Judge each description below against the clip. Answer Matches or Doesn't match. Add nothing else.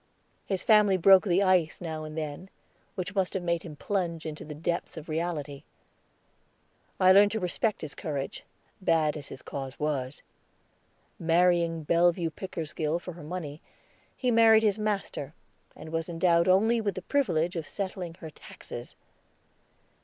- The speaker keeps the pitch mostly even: Doesn't match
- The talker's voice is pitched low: Doesn't match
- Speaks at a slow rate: Doesn't match